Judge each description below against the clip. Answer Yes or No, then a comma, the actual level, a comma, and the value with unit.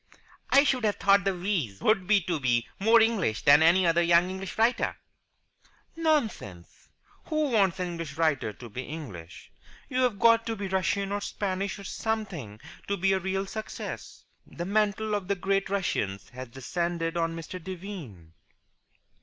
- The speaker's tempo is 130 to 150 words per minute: No, average, 160 wpm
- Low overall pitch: No, high, 190 Hz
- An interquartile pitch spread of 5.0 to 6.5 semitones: No, average, 4.3 semitones